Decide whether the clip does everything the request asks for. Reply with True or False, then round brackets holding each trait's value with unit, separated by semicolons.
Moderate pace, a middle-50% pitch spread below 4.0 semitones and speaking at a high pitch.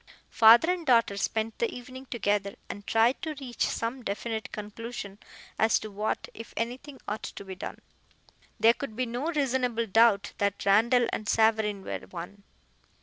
True (160 wpm; 3.1 semitones; 225 Hz)